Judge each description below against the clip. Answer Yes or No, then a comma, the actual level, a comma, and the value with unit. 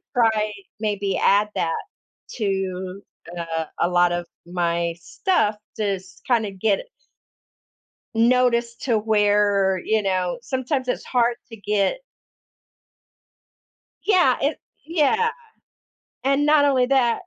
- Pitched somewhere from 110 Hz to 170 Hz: No, high, 210 Hz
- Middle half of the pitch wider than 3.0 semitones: Yes, average, 4.9 semitones